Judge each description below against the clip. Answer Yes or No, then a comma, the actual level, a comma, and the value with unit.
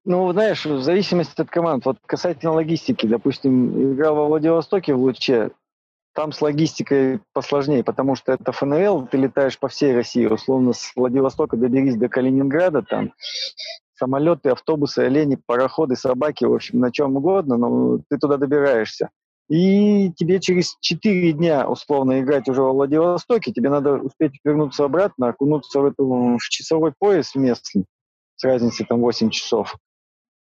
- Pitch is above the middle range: No, medium, 140 Hz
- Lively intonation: No, average, 3.9 semitones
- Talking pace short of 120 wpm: No, average, 150 wpm